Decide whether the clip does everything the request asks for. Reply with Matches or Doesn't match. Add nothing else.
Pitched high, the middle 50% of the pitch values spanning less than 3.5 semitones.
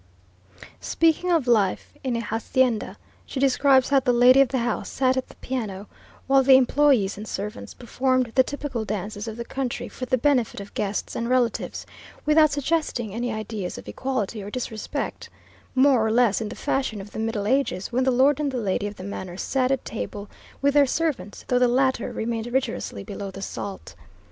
Doesn't match